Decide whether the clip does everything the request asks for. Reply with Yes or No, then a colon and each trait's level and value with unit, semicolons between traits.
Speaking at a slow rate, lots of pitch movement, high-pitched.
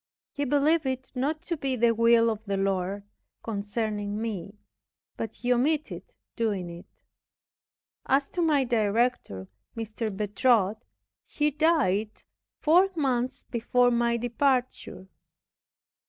No: slow, 115 wpm; average, 4.6 semitones; high, 235 Hz